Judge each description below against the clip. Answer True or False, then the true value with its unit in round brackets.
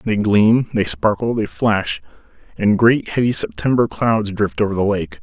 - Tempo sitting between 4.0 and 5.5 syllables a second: True (4.4 syllables/s)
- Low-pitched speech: True (105 Hz)